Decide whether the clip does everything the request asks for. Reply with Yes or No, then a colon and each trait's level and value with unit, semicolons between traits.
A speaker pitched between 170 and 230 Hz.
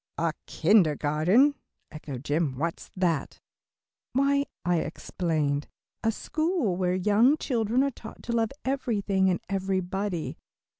Yes: high, 190 Hz